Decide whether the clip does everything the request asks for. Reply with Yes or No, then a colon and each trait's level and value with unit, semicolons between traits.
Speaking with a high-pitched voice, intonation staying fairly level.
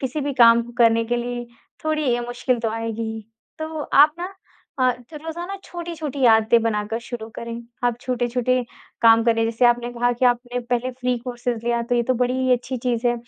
Yes: high, 245 Hz; narrow, 1.8 semitones